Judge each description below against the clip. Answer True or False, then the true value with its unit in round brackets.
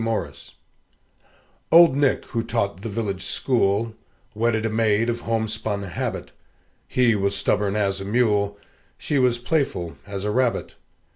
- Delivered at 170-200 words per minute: False (140 wpm)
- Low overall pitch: True (110 Hz)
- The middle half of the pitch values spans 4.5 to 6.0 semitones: False (2.8 semitones)